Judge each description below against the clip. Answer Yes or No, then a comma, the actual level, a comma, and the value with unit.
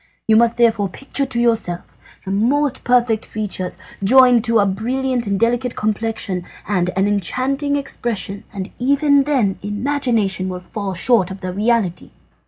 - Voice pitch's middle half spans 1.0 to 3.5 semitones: No, average, 4.3 semitones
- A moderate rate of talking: Yes, average, 150 wpm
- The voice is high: Yes, high, 225 Hz